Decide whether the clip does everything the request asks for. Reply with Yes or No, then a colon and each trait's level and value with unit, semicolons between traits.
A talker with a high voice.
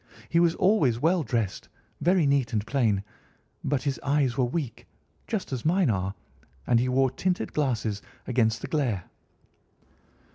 No: low, 130 Hz